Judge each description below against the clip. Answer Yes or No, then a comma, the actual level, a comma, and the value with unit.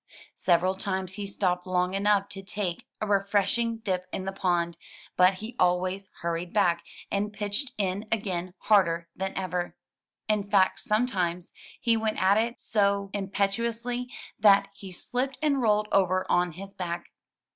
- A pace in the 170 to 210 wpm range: No, average, 155 wpm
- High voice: Yes, high, 195 Hz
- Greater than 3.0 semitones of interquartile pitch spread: No, narrow, 2.6 semitones